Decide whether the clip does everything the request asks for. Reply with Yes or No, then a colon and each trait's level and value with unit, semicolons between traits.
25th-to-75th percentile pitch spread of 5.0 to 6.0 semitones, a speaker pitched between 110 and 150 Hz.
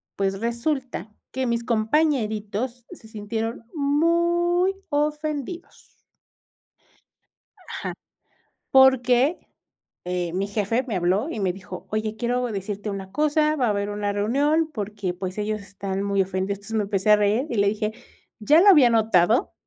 No: wide, 5.4 semitones; high, 220 Hz